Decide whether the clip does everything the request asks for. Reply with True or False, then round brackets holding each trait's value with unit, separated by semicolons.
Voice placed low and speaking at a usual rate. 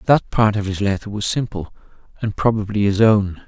True (105 Hz; 190 wpm)